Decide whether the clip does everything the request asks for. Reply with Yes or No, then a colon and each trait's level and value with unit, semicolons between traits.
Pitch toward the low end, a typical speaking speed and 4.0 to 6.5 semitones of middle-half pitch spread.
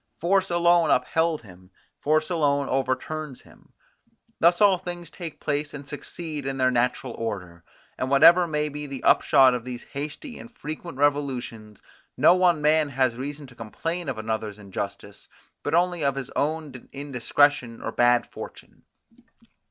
No: medium, 145 Hz; average, 150 wpm; average, 4.4 semitones